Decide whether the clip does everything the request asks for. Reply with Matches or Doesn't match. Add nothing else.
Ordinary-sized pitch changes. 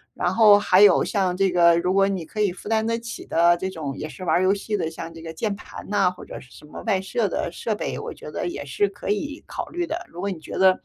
Matches